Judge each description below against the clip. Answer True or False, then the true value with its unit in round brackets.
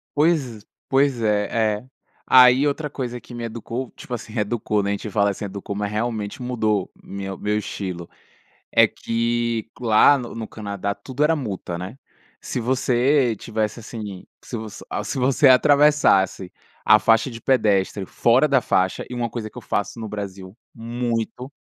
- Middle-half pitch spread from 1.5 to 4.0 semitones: True (3.5 semitones)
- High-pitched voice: False (115 Hz)